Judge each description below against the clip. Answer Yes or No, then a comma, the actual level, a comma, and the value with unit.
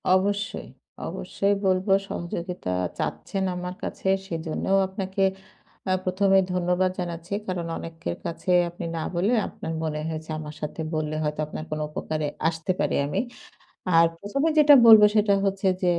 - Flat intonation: No, average, 3.1 semitones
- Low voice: No, medium, 180 Hz